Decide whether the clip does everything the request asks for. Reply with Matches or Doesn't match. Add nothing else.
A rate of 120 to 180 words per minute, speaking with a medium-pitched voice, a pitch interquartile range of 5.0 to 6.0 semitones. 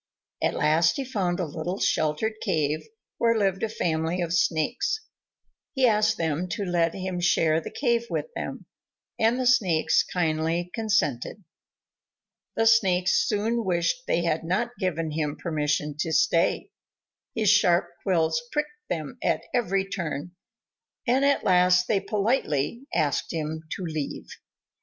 Matches